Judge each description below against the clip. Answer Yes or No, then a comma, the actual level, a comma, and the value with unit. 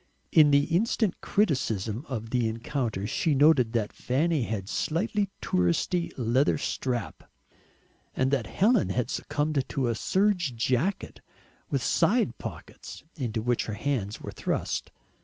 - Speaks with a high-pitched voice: No, low, 130 Hz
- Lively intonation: Yes, wide, 6.1 semitones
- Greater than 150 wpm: No, average, 140 wpm